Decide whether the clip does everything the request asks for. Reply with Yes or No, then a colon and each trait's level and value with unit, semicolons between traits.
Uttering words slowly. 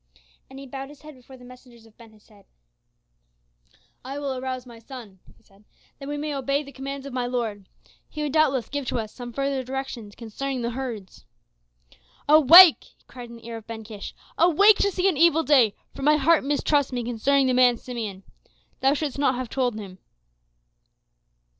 No: average, 190 wpm